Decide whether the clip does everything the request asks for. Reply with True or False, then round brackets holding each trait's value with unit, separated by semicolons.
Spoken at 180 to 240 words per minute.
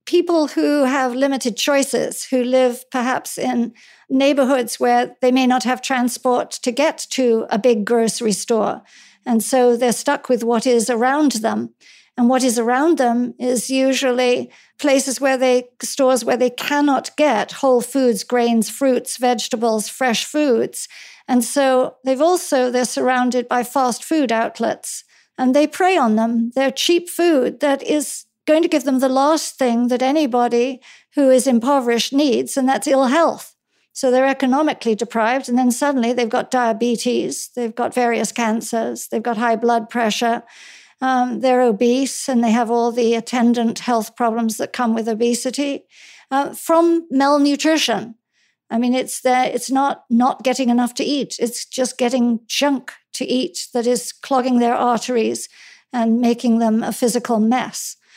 False (160 wpm)